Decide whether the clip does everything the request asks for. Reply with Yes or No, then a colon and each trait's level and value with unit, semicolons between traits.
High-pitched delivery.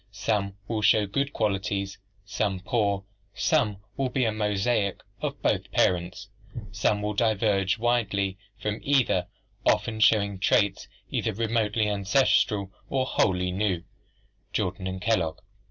No: low, 105 Hz